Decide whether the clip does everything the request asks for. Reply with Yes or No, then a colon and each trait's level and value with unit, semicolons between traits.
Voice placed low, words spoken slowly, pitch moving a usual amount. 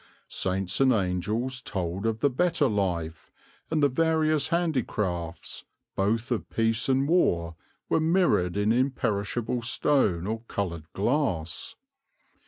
No: low, 115 Hz; slow, 120 wpm; wide, 6.7 semitones